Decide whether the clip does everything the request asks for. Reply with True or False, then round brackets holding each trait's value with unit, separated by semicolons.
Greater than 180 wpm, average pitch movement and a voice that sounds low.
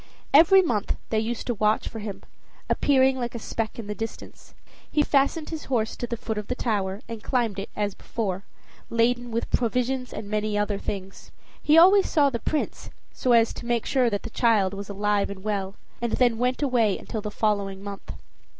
False (200 wpm; 3.3 semitones; 225 Hz)